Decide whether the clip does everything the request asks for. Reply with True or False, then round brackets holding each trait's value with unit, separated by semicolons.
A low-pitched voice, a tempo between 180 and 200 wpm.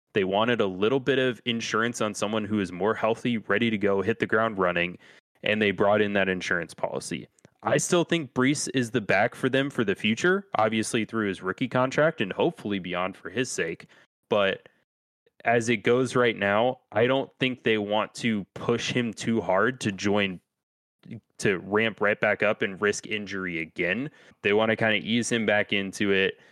True (110 Hz; 195 wpm)